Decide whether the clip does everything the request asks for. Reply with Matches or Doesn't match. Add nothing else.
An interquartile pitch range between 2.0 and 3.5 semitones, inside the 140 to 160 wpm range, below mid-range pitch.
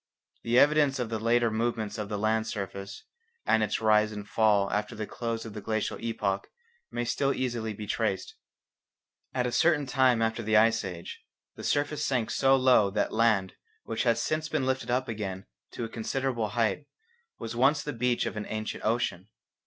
Doesn't match